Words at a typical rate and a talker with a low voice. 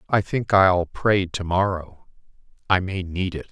Yes: average, 170 wpm; very low, 90 Hz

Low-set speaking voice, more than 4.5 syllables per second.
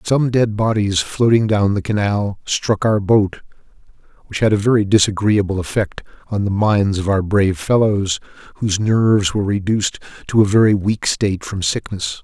Yes: low, 105 Hz; 5.1 syllables/s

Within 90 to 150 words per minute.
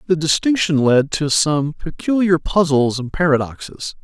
Yes: slow, 135 wpm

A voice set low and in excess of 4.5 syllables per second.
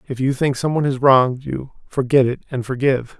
Yes: low, 130 Hz; 5.8 syllables/s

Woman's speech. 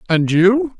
No: male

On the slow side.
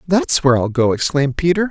No: fast, 210 wpm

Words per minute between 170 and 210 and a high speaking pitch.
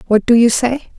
No: fast, 245 wpm; high, 240 Hz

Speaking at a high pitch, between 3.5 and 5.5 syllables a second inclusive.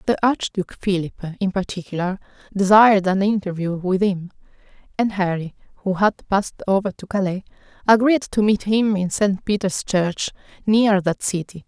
Yes: high, 195 Hz; 5.0 syllables/s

